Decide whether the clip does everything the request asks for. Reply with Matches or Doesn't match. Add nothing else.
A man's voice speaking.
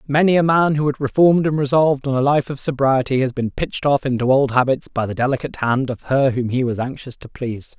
Matches